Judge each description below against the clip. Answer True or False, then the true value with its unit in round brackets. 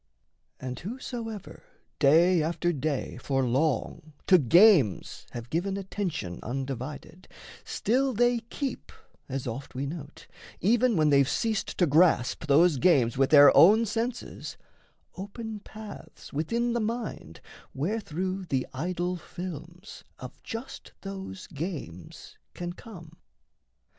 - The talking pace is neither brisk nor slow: False (120 wpm)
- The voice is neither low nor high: True (175 Hz)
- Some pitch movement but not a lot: False (7.0 semitones)